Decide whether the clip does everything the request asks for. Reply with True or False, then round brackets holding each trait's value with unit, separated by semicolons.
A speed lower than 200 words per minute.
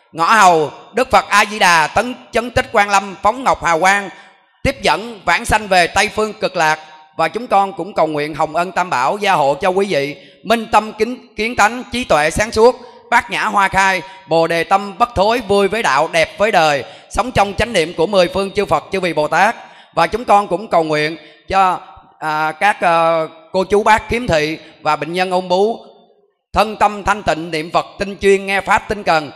False (225 wpm)